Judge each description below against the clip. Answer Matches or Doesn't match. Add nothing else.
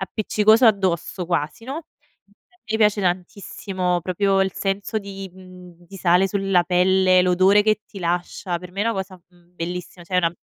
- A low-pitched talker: Doesn't match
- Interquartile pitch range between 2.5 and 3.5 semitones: Doesn't match